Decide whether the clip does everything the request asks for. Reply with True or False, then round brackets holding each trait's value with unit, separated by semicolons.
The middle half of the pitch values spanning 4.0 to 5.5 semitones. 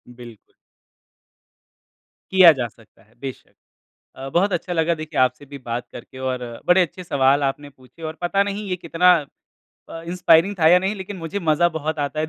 True (4.8 semitones)